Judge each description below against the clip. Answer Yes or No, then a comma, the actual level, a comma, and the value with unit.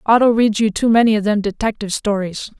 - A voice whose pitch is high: Yes, high, 215 Hz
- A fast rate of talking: Yes, fast, 210 wpm